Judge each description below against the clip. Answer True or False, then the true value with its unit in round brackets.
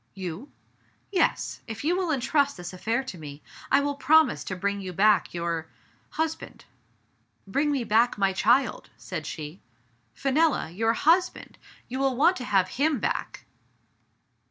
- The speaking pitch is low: False (240 Hz)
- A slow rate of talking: False (155 wpm)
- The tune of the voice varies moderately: False (7.3 semitones)